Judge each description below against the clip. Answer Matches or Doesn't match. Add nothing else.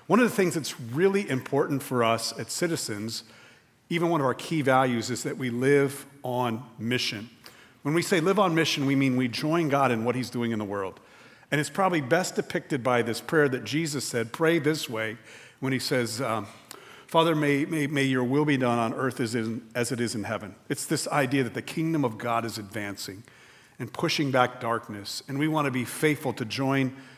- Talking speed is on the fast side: Matches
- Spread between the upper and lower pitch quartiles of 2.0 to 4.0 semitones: Doesn't match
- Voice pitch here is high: Doesn't match